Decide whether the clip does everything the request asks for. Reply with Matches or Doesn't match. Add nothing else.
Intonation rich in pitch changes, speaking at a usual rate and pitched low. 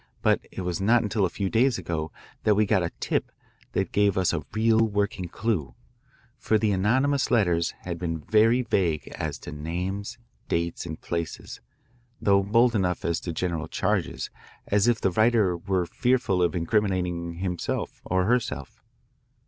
Doesn't match